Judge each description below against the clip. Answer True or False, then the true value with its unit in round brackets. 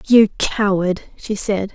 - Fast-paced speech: False (140 wpm)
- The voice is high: True (200 Hz)